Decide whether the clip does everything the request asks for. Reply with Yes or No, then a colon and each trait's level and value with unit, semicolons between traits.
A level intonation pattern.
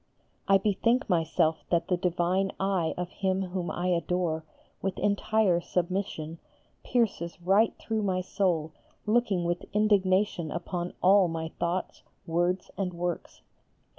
Yes: narrow, 2.3 semitones